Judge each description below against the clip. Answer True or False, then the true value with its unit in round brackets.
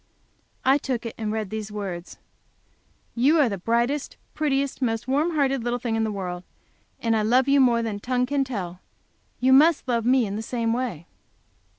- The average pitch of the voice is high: True (235 Hz)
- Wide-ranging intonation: False (3.6 semitones)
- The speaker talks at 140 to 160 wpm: False (190 wpm)